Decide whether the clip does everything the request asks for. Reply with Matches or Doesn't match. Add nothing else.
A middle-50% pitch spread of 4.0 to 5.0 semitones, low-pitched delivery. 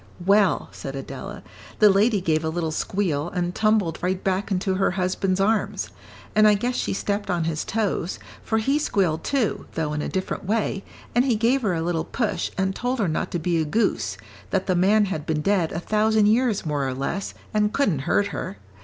Doesn't match